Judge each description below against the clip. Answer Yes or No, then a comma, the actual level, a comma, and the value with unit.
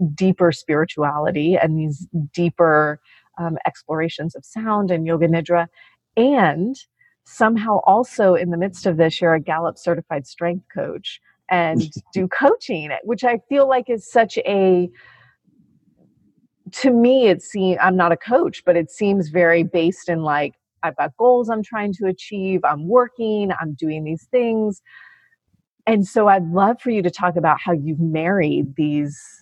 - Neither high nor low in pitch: Yes, medium, 180 Hz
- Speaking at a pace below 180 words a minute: Yes, average, 155 wpm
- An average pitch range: Yes, average, 4.9 semitones